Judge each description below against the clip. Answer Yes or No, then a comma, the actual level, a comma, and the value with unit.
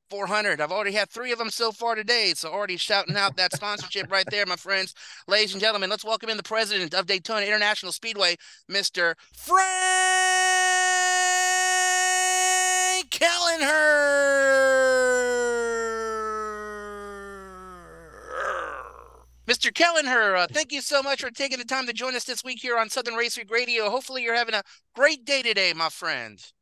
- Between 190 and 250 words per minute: No, average, 150 wpm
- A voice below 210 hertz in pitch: No, high, 230 Hz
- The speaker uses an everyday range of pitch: No, wide, 5.8 semitones